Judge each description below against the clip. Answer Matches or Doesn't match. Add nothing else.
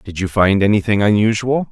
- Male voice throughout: Matches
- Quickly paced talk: Doesn't match